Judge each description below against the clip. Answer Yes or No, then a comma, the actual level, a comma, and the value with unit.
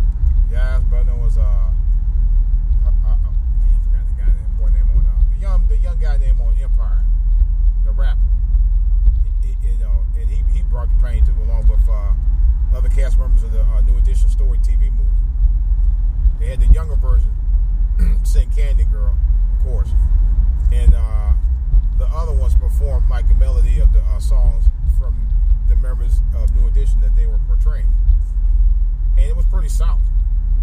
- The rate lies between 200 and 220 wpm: No, average, 170 wpm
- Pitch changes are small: Yes, narrow, 1.7 semitones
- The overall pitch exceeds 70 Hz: No, very low, 65 Hz